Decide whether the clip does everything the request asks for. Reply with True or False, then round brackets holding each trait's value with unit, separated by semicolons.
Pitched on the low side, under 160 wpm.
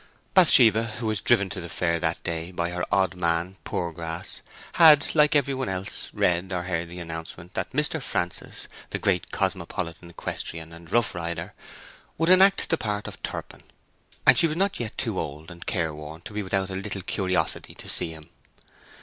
False (90 Hz; 175 wpm)